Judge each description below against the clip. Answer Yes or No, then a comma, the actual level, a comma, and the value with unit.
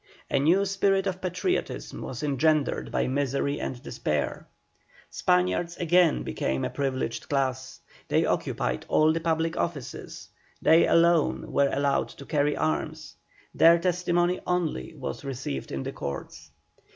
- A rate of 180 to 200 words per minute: No, slow, 135 wpm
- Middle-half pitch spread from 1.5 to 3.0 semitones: No, average, 4.7 semitones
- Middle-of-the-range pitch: Yes, medium, 150 Hz